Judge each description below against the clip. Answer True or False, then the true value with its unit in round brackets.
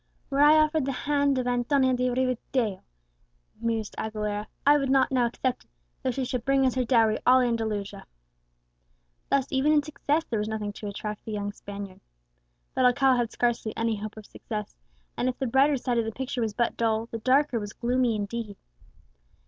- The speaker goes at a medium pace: True (190 wpm)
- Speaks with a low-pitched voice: False (245 Hz)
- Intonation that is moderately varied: True (3.4 semitones)